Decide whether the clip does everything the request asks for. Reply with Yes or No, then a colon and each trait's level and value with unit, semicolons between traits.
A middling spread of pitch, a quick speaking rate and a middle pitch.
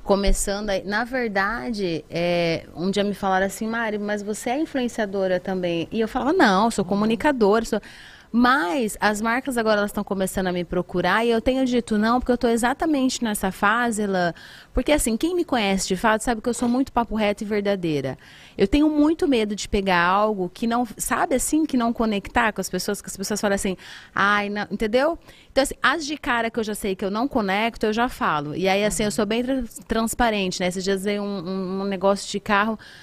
No: average, 3.7 semitones; fast, 210 wpm; high, 215 Hz